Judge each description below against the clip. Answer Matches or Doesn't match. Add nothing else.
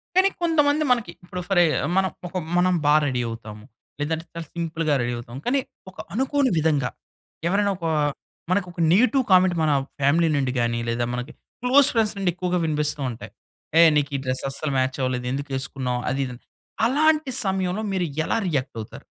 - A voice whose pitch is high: Doesn't match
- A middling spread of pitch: Doesn't match